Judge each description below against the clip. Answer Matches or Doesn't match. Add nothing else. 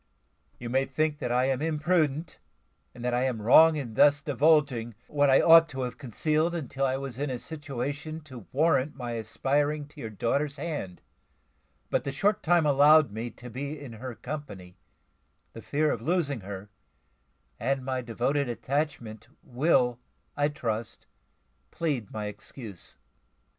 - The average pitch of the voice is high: Doesn't match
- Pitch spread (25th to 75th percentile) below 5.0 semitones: Matches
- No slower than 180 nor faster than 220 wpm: Doesn't match